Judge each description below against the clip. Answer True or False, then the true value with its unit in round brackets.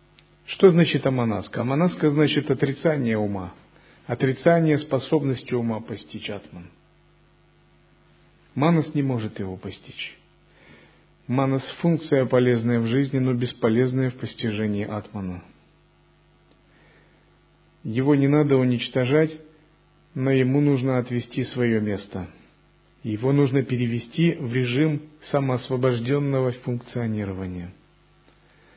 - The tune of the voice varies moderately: True (3.8 semitones)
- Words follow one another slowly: True (90 wpm)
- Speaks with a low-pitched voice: True (130 Hz)